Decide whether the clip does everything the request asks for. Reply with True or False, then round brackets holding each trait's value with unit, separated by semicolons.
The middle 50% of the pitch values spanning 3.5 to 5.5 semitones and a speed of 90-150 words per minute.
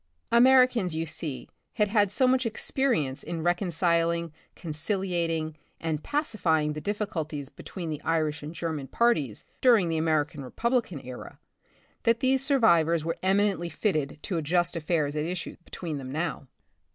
True (5.1 semitones; 145 wpm)